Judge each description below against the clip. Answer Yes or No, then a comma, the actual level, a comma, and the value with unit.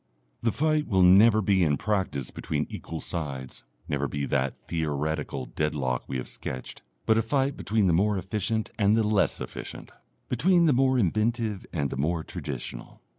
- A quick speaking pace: No, average, 170 wpm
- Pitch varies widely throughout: Yes, wide, 7.2 semitones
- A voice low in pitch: Yes, very low, 95 Hz